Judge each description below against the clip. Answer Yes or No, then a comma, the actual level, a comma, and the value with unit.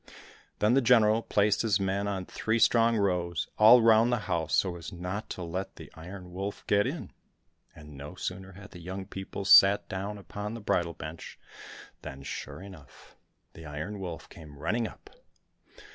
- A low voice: Yes, very low, 95 Hz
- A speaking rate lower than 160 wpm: No, average, 175 wpm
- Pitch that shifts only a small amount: No, average, 3.3 semitones